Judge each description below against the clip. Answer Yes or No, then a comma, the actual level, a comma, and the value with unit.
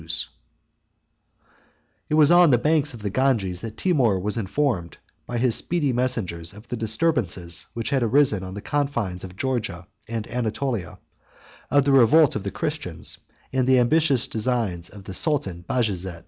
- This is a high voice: No, low, 115 Hz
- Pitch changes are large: Yes, wide, 6.0 semitones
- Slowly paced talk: No, average, 160 wpm